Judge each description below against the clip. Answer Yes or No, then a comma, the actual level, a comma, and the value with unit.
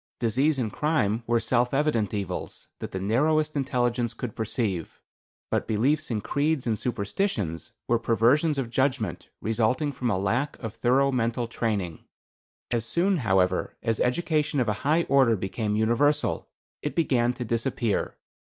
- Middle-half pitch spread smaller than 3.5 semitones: No, average, 4.4 semitones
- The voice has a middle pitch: No, low, 120 Hz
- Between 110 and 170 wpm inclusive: Yes, average, 150 wpm